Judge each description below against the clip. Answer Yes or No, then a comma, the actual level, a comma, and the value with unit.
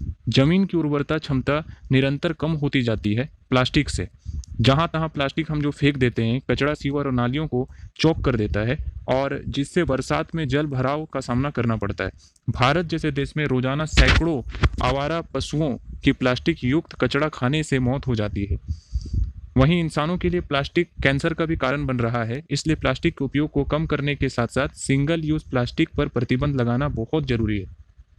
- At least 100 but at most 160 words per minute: No, average, 185 wpm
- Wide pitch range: No, average, 3.9 semitones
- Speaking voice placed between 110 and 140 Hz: Yes, low, 135 Hz